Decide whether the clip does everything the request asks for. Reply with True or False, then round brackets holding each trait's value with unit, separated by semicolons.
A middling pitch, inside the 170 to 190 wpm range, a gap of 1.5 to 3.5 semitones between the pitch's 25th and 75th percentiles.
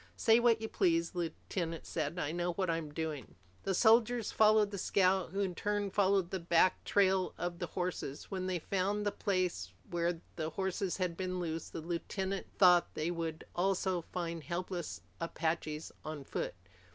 True (180 Hz; 175 wpm; 2.7 semitones)